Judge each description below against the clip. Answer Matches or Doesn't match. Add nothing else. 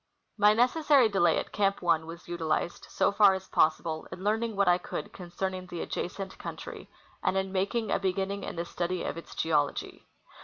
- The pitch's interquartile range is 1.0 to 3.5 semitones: Matches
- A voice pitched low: Doesn't match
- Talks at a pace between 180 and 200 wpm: Matches